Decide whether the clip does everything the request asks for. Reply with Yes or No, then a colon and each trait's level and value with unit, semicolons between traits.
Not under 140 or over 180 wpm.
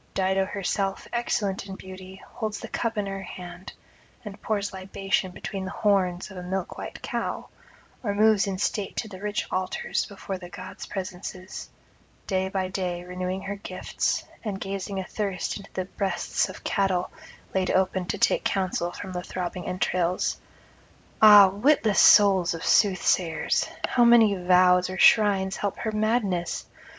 Yes: average, 155 wpm